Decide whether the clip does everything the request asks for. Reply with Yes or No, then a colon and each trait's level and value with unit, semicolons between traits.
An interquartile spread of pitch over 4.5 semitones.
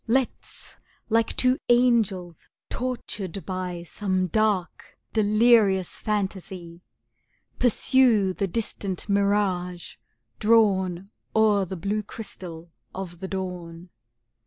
No: average, 3.2 semitones